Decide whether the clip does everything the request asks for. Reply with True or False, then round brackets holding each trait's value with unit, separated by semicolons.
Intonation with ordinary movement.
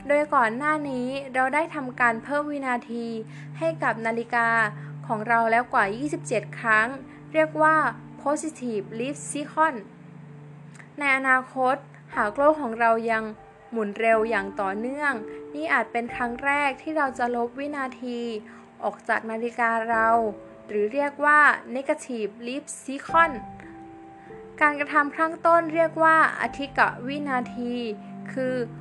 True (4.5 semitones)